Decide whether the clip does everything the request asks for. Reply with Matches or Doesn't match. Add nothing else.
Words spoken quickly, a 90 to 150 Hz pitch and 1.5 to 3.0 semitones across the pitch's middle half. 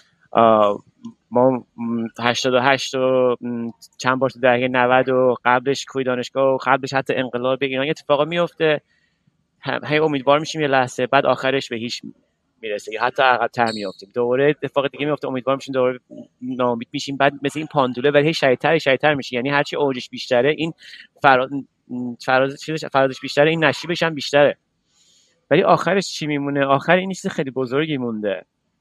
Matches